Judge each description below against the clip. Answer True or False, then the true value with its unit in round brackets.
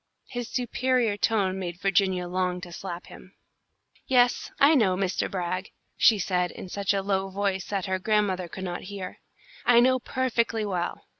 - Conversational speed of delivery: True (165 wpm)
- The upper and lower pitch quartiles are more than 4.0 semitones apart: False (3.5 semitones)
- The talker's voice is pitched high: True (195 Hz)